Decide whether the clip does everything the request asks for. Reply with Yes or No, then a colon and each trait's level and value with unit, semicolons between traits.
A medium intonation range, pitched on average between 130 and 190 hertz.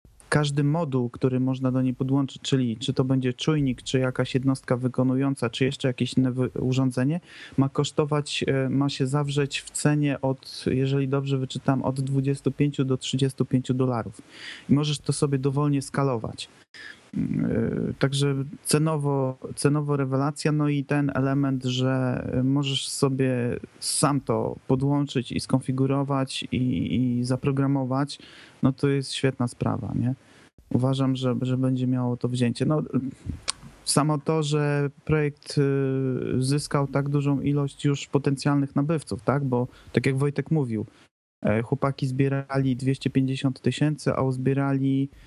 No: narrow, 1.7 semitones; low, 135 Hz